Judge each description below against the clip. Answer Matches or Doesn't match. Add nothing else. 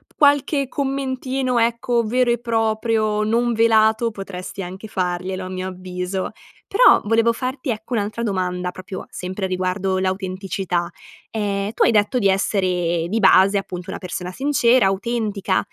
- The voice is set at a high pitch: Matches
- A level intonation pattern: Doesn't match